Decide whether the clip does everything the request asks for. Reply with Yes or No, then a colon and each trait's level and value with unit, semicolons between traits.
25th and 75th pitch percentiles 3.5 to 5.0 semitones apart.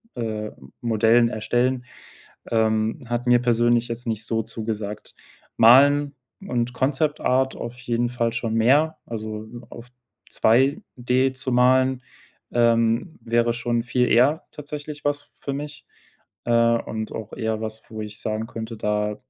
No: narrow, 2.6 semitones